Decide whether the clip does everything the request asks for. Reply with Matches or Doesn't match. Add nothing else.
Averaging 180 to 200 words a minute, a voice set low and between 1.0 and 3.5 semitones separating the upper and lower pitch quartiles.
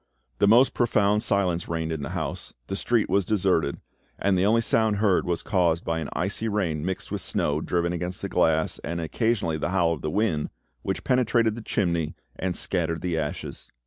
Doesn't match